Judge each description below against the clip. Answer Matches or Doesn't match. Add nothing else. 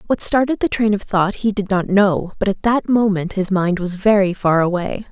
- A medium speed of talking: Doesn't match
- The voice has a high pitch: Matches